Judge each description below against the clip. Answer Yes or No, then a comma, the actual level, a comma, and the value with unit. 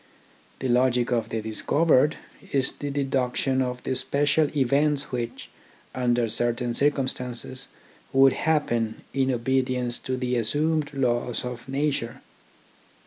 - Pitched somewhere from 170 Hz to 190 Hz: No, low, 130 Hz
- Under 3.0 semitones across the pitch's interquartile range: Yes, narrow, 2.4 semitones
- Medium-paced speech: No, slow, 125 wpm